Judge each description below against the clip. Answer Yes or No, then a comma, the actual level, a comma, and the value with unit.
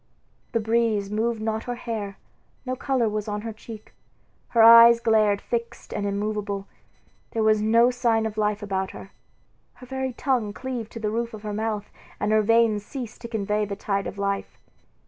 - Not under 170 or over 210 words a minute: Yes, average, 185 wpm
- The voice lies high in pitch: Yes, high, 220 Hz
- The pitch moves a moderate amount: No, narrow, 2.0 semitones